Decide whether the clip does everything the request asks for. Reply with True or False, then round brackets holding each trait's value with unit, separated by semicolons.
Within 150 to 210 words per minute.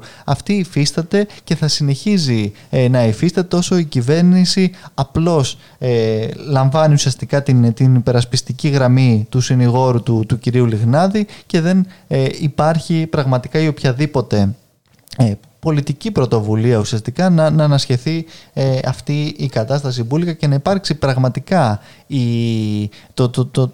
False (140 wpm)